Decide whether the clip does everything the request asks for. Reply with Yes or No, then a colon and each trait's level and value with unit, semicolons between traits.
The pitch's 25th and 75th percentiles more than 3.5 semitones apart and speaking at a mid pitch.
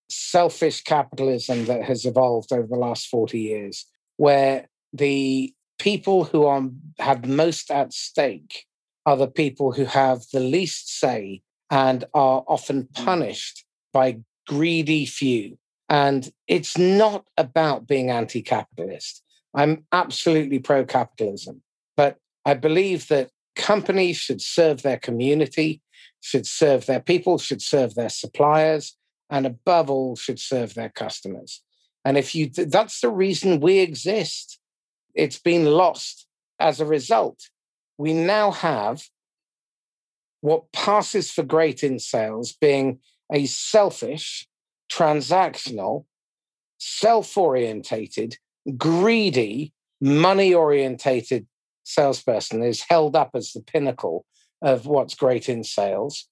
Yes: average, 3.9 semitones; medium, 145 Hz